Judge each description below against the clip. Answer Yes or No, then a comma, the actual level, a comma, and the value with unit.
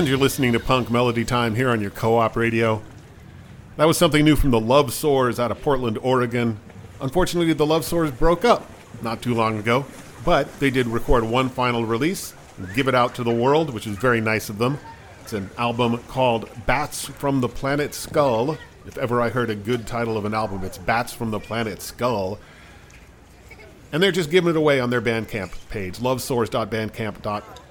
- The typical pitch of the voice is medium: No, low, 120 Hz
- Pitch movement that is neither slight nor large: Yes, average, 3.4 semitones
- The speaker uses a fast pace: No, average, 195 wpm